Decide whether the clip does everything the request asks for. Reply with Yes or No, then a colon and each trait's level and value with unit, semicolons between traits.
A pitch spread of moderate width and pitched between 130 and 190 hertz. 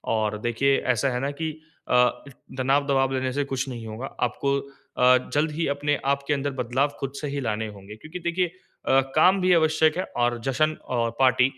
Yes: average, 3.5 semitones; medium, 140 Hz